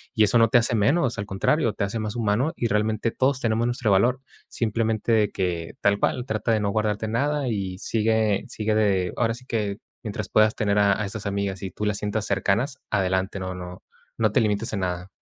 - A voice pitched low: Yes, low, 105 Hz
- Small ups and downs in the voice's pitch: Yes, narrow, 2.3 semitones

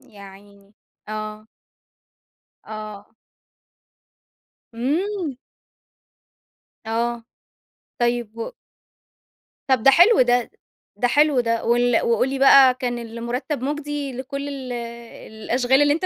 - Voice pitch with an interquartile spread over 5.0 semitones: No, average, 3.3 semitones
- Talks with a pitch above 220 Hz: Yes, high, 245 Hz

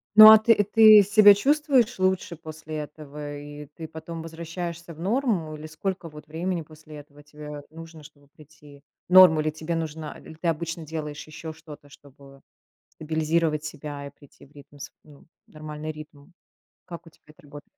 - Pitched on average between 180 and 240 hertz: No, medium, 155 Hz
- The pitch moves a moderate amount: No, narrow, 2.2 semitones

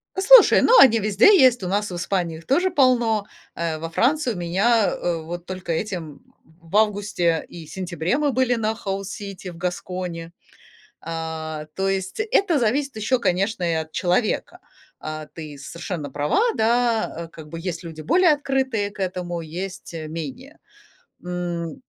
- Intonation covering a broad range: Yes, wide, 5.7 semitones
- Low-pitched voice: No, medium, 185 Hz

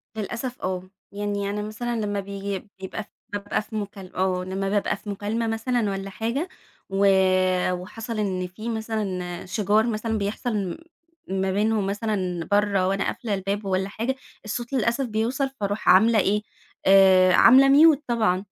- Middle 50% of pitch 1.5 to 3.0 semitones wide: Yes, narrow, 2.5 semitones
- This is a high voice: Yes, high, 205 Hz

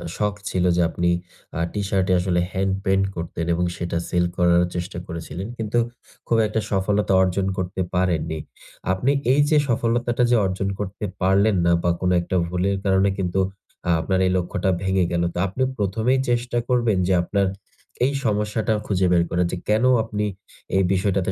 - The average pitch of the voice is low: Yes, very low, 95 Hz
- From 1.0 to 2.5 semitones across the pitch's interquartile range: No, average, 2.9 semitones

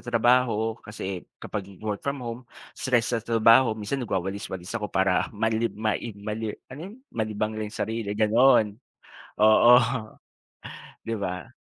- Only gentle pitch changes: Yes, narrow, 2.0 semitones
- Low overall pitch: Yes, low, 110 Hz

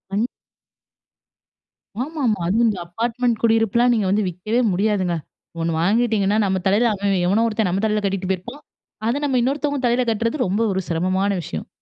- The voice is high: Yes, high, 215 Hz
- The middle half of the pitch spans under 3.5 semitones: No, average, 3.8 semitones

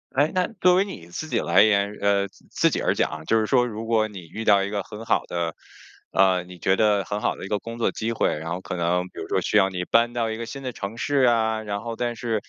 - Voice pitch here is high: No, low, 105 Hz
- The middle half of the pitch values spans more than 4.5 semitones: No, average, 3.3 semitones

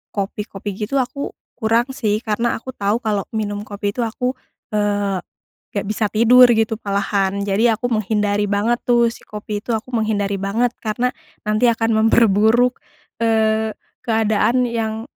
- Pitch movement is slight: Yes, narrow, 2.2 semitones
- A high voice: Yes, high, 220 Hz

